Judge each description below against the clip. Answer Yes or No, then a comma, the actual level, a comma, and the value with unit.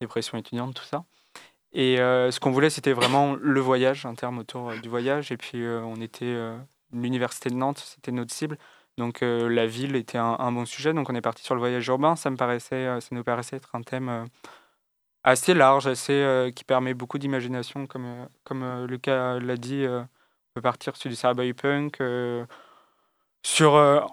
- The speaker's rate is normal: Yes, average, 210 wpm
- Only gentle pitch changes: Yes, narrow, 2.0 semitones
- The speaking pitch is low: Yes, low, 125 Hz